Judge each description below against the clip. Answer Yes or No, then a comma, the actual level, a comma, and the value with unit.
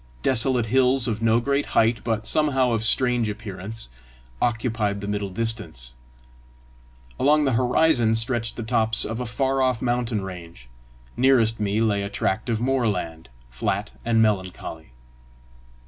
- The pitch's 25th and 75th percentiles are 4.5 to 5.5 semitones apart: No, average, 3.2 semitones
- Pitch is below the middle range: Yes, low, 115 Hz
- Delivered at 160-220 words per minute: No, average, 140 wpm